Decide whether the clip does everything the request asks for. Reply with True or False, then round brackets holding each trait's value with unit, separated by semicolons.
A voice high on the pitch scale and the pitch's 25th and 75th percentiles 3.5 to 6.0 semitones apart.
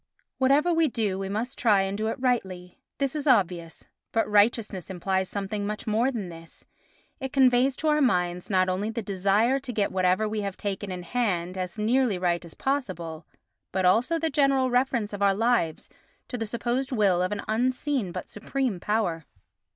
True (210 Hz; 5.2 semitones)